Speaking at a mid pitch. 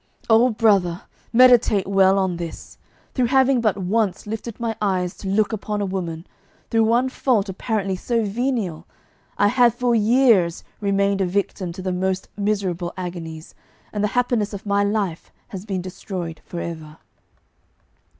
No: high, 200 Hz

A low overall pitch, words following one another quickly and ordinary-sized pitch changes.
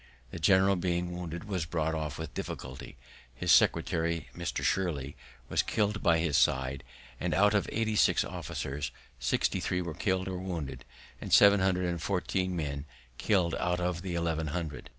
No: very low, 85 Hz; average, 165 wpm; average, 3.2 semitones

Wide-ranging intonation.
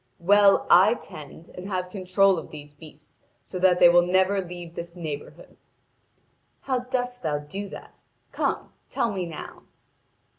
No: average, 2.9 semitones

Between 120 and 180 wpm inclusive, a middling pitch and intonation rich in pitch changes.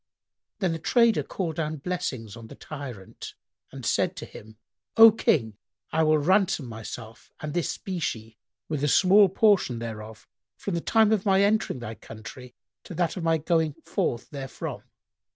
Yes: average, 165 wpm; medium, 155 Hz; wide, 8.1 semitones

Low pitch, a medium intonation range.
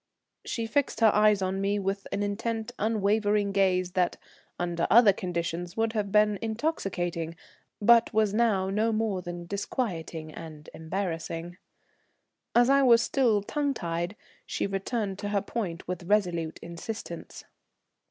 No: high, 200 Hz; average, 3.9 semitones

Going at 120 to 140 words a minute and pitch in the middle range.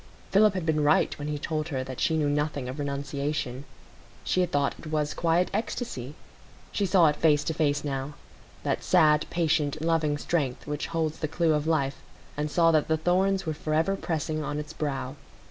No: average, 185 wpm; medium, 155 Hz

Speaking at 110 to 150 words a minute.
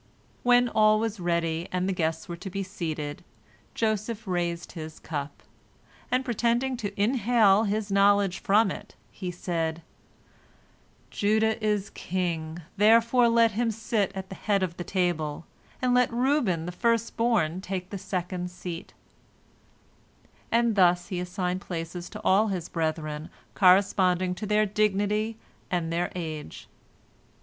Yes: average, 140 wpm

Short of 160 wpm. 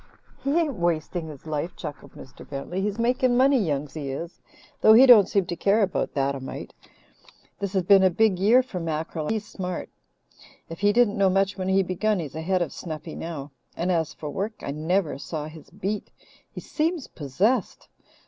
No: average, 195 wpm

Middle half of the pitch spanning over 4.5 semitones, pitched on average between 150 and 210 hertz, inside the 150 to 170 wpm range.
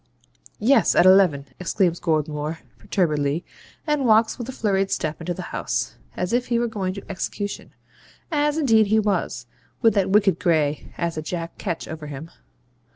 Yes: wide, 5.4 semitones; high, 190 Hz; average, 165 wpm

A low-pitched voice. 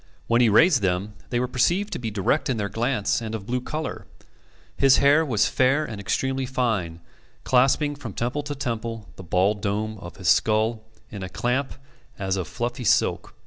Yes: low, 115 Hz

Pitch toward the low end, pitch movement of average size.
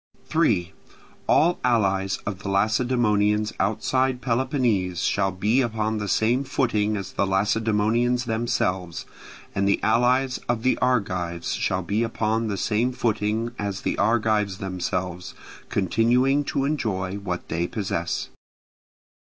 Yes: low, 110 Hz; average, 3.7 semitones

